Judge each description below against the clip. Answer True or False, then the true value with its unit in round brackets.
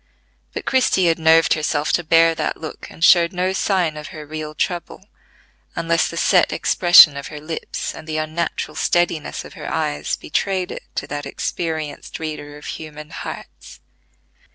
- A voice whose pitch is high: False (160 Hz)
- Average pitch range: False (2.3 semitones)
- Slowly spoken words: False (165 wpm)